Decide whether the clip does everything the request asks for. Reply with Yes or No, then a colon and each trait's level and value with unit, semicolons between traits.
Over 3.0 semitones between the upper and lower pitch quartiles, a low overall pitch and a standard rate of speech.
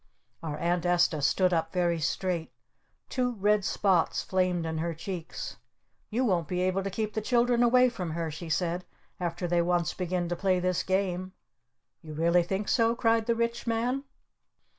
No: average, 4.0 semitones; medium, 180 Hz; average, 175 wpm